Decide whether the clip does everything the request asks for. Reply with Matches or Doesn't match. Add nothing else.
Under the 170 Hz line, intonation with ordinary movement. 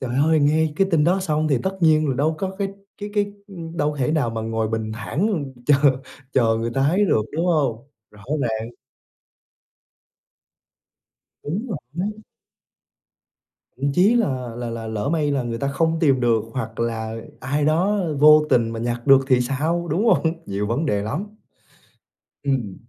Doesn't match